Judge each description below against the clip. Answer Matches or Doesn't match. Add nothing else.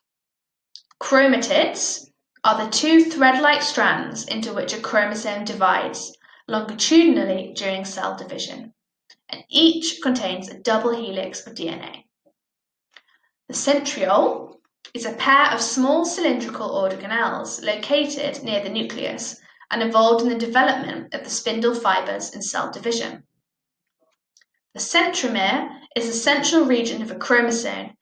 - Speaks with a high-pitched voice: Matches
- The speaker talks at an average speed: Doesn't match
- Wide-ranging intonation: Doesn't match